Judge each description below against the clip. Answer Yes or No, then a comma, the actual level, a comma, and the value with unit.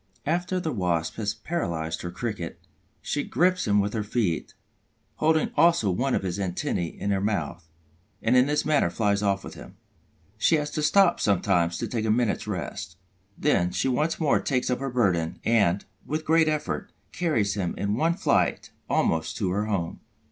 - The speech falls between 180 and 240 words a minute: Yes, average, 185 wpm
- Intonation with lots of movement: Yes, wide, 8.1 semitones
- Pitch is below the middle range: Yes, low, 110 Hz